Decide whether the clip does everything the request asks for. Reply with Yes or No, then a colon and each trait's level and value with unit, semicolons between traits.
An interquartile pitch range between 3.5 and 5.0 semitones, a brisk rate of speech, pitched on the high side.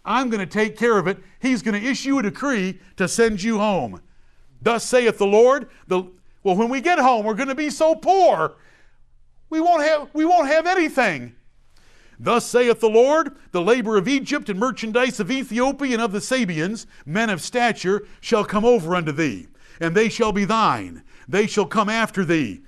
No: average, 4.4 semitones; average, 195 wpm; high, 230 Hz